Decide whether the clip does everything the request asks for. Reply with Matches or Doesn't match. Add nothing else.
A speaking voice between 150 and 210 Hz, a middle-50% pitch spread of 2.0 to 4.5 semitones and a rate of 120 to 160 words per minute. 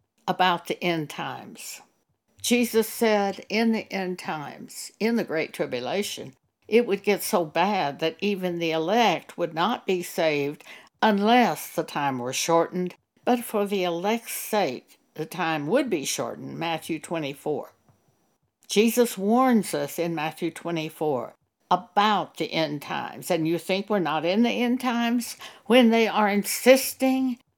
Doesn't match